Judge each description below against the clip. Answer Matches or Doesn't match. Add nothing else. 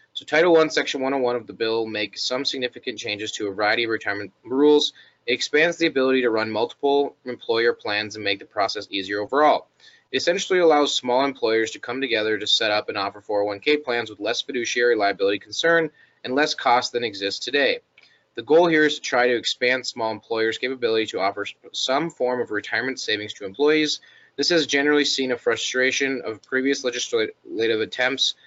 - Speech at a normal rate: Matches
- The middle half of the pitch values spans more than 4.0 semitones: Matches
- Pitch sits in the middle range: Doesn't match